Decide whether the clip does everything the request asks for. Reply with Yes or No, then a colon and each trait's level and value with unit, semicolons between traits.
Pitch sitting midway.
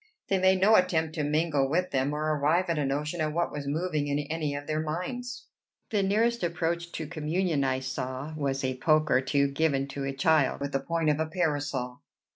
Yes: medium, 155 Hz